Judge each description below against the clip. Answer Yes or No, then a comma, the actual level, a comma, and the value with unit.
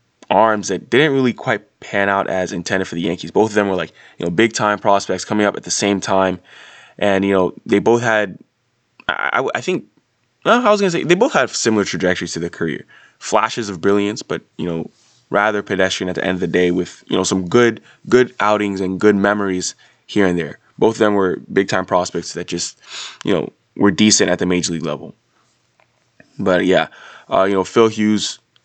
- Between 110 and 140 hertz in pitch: No, low, 100 Hz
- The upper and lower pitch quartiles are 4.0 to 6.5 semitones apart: No, average, 2.8 semitones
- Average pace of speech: No, fast, 215 wpm